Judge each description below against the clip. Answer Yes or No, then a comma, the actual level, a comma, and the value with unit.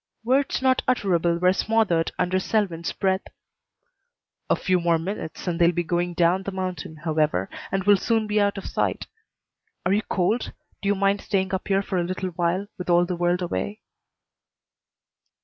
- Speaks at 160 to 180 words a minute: Yes, average, 175 wpm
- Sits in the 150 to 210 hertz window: Yes, medium, 185 Hz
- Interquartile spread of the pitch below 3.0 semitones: Yes, narrow, 2.6 semitones